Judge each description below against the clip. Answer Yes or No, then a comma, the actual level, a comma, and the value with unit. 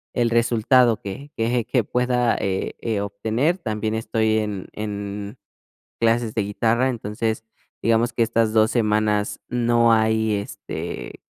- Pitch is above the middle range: No, low, 110 Hz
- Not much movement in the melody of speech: Yes, narrow, 1.9 semitones